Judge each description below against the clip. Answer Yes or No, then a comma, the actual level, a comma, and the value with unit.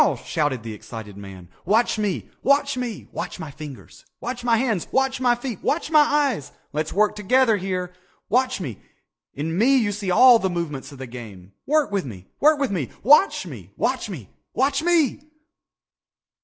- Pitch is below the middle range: No, high, 205 Hz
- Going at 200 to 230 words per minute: No, average, 175 wpm